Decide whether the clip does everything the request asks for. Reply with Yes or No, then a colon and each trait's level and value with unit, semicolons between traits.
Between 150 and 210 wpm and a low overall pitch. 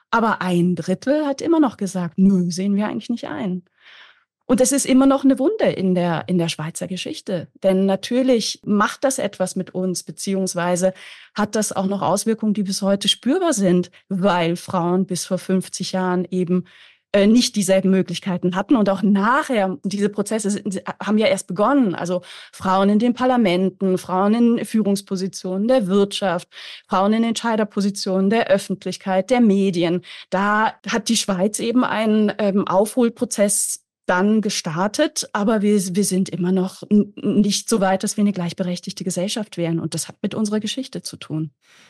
No: average, 160 wpm; high, 195 Hz